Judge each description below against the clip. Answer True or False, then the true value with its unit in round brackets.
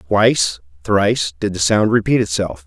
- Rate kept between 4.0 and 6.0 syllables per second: True (4.9 syllables/s)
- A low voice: True (95 Hz)